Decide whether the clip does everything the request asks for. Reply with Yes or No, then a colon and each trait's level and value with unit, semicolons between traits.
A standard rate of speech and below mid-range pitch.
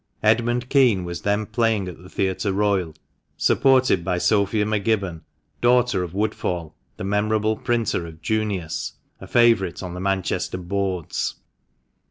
Yes: average, 145 wpm; low, 100 Hz